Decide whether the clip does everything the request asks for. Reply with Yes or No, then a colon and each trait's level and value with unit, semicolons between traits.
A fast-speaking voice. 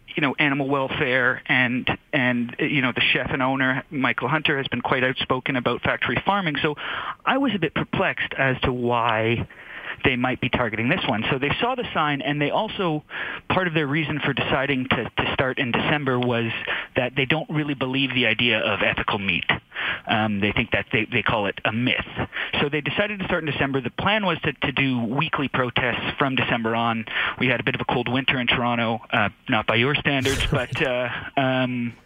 Yes: fast, 210 wpm